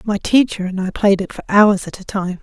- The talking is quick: Yes, fast, 270 wpm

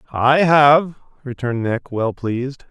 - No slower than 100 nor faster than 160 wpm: Yes, slow, 135 wpm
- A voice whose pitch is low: Yes, low, 130 Hz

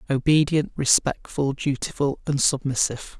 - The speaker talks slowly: Yes, slow, 95 wpm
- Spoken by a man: Yes, male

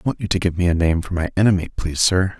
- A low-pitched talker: Yes, very low, 90 Hz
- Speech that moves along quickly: Yes, fast, 325 wpm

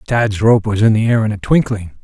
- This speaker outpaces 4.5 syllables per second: Yes, 5.5 syllables/s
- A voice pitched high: No, low, 110 Hz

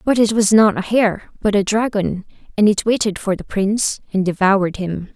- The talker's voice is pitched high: Yes, high, 205 Hz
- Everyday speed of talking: No, fast, 210 wpm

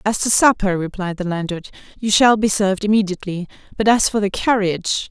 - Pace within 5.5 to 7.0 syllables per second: Yes, 5.9 syllables/s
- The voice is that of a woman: Yes, female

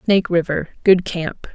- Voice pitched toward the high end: No, medium, 175 Hz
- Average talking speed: No, slow, 115 wpm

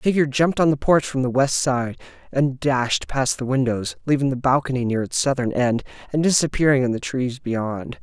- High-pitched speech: No, low, 130 Hz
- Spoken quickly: Yes, fast, 210 wpm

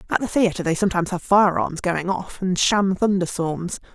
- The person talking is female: Yes, female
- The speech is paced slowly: No, average, 200 wpm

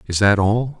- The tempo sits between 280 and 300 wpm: No, fast, 225 wpm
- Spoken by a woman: No, male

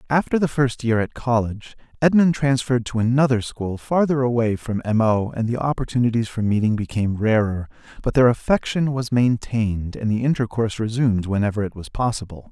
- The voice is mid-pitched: No, low, 120 Hz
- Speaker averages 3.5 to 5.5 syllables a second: No, 5.9 syllables/s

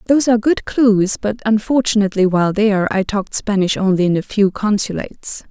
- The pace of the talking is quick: No, average, 175 wpm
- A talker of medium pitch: No, high, 210 Hz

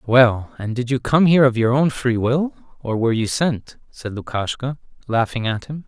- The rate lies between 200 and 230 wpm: Yes, fast, 205 wpm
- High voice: No, low, 125 Hz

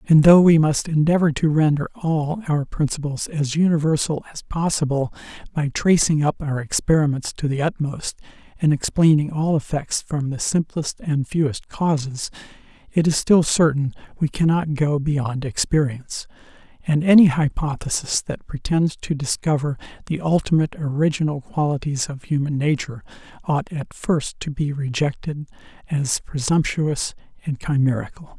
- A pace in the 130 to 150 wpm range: Yes, slow, 135 wpm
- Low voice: No, medium, 150 Hz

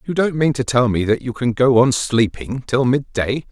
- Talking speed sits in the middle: No, fast, 255 wpm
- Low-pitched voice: Yes, low, 125 Hz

